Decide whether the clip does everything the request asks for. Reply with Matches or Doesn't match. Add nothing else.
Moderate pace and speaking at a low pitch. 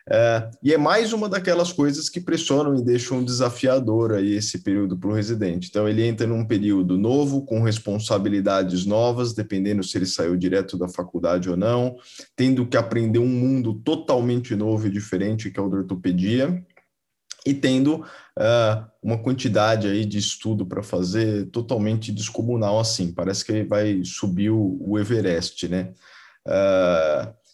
Matches